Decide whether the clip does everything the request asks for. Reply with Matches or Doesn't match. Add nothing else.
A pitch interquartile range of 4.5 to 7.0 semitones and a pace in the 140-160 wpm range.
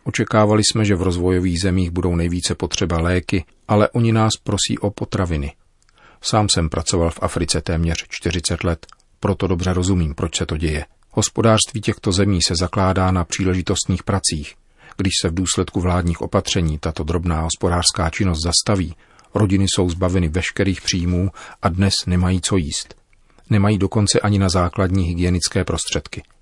Doesn't match